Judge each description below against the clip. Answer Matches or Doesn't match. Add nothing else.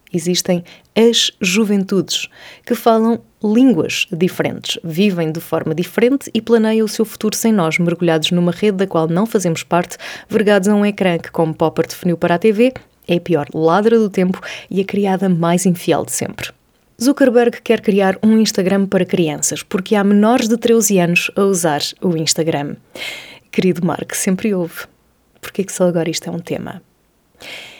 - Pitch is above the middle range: Matches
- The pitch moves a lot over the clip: Doesn't match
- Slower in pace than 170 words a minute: Doesn't match